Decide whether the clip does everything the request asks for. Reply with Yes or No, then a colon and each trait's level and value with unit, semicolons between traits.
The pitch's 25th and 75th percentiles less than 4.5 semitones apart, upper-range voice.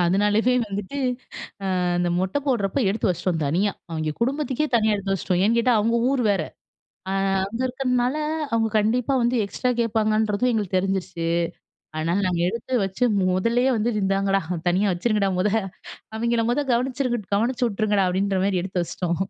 Yes: average, 4.0 semitones; high, 210 Hz